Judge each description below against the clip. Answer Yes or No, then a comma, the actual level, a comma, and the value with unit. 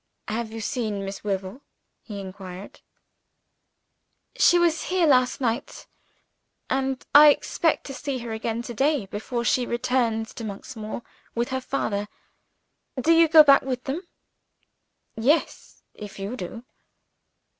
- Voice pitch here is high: Yes, high, 240 Hz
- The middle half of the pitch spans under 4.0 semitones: No, average, 4.4 semitones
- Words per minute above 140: No, slow, 135 wpm